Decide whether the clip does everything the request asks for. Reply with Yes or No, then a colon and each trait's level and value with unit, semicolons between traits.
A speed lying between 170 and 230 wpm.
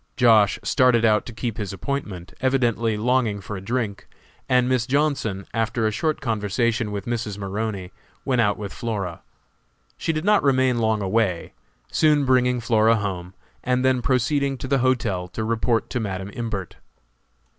No: average, 160 wpm